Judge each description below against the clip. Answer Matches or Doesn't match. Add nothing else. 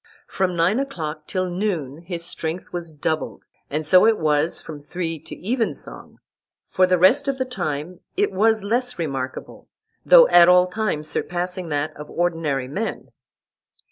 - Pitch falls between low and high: Matches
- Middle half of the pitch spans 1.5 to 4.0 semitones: Doesn't match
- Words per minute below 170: Matches